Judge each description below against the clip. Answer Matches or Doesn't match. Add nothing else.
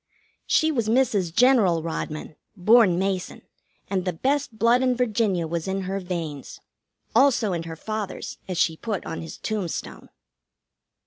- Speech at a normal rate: Matches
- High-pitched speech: Matches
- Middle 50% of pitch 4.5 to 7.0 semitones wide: Matches